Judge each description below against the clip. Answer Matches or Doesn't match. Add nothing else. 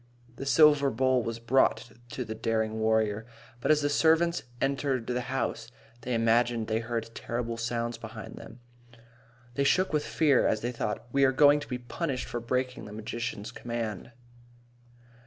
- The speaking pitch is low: Matches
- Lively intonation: Doesn't match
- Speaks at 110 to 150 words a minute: Doesn't match